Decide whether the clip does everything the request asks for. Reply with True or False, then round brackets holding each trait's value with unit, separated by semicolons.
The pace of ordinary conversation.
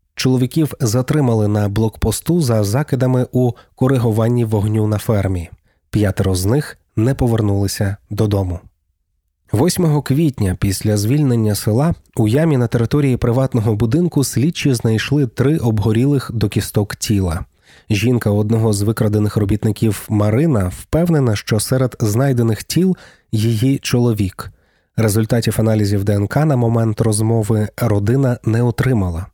True (115 wpm)